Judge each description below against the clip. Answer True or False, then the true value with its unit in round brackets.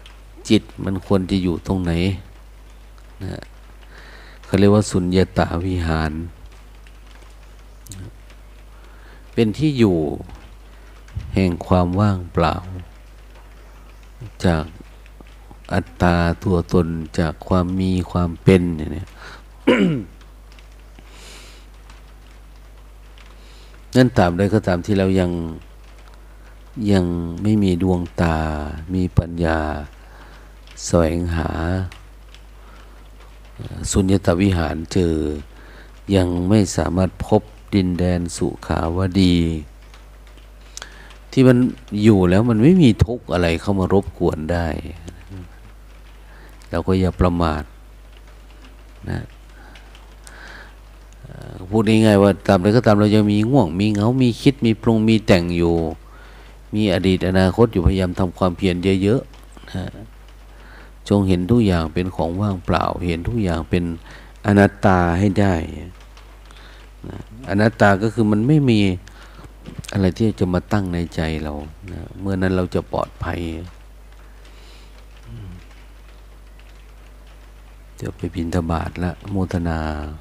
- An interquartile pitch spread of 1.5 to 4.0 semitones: True (3.5 semitones)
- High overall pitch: False (95 Hz)